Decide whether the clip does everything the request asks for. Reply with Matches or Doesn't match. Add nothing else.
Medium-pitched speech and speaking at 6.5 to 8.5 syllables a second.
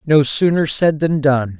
Doesn't match